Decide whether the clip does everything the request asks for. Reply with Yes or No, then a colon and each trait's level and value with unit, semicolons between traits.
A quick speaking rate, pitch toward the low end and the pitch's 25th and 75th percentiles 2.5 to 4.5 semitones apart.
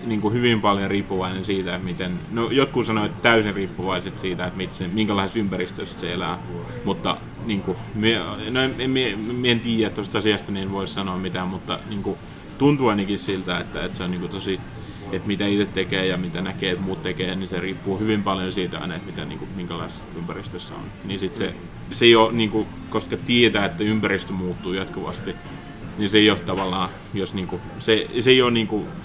Yes: fast, 205 wpm; low, 100 Hz; average, 2.9 semitones